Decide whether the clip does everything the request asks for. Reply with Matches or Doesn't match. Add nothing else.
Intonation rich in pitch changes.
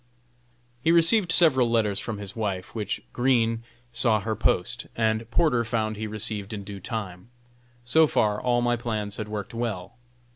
Doesn't match